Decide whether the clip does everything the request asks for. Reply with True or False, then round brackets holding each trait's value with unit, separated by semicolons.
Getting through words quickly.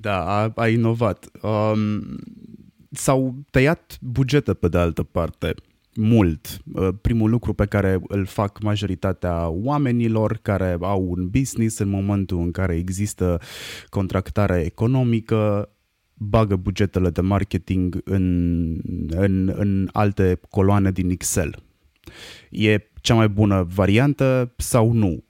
False (120 wpm)